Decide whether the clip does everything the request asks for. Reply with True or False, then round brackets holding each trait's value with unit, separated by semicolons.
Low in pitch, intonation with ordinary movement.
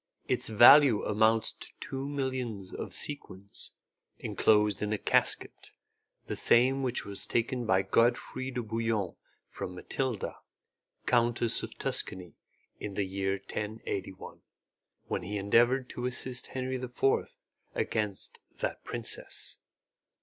True (115 Hz; 3.9 semitones)